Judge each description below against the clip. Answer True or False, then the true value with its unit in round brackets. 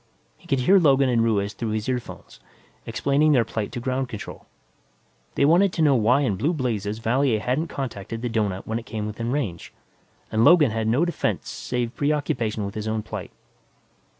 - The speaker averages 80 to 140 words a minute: False (185 wpm)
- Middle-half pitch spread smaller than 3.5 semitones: False (4.3 semitones)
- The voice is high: False (120 Hz)